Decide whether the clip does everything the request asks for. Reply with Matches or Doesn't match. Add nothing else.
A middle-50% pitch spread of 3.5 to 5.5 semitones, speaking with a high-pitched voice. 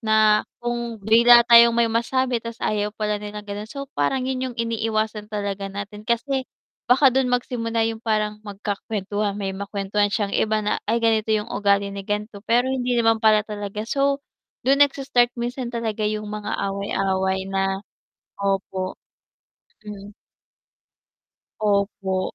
Doesn't match